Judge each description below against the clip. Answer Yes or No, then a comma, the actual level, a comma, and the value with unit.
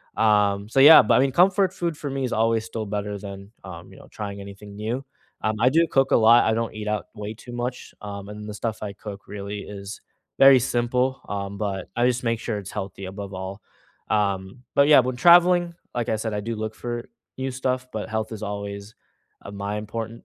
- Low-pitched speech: Yes, low, 110 Hz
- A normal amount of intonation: Yes, average, 3.7 semitones